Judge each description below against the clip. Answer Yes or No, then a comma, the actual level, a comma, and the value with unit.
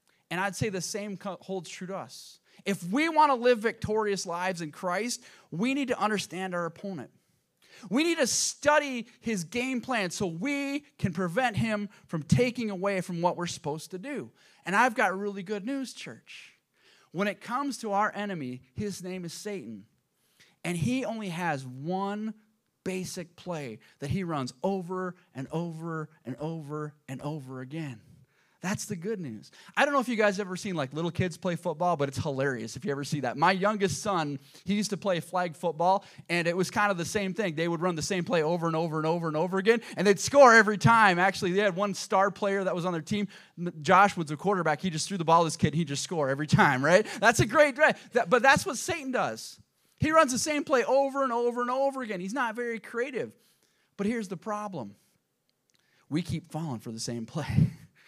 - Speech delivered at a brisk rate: Yes, fast, 215 wpm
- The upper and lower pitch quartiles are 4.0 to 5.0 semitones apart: Yes, average, 4.7 semitones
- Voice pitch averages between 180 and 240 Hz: Yes, high, 190 Hz